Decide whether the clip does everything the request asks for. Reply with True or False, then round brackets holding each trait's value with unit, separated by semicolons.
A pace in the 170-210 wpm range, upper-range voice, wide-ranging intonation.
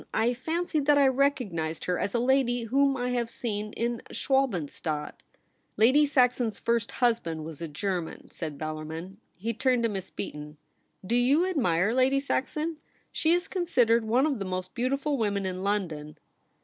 True (175 wpm; 235 Hz; 6.5 semitones)